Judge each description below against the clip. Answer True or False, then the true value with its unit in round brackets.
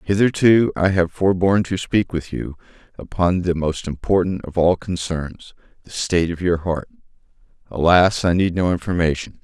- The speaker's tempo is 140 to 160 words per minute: True (155 wpm)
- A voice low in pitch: True (90 Hz)